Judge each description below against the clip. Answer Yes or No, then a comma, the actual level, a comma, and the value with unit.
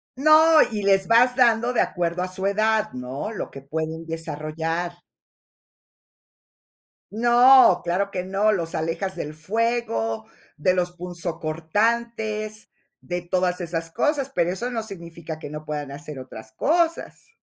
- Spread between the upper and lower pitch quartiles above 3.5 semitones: Yes, wide, 5.5 semitones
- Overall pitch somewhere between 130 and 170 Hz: No, medium, 180 Hz